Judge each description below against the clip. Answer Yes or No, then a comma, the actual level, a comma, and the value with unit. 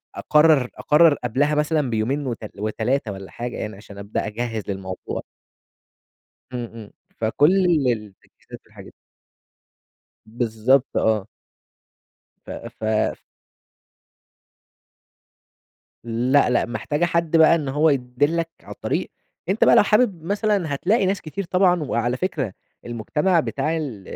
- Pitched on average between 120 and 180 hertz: Yes, low, 135 Hz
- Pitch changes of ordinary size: No, wide, 6.5 semitones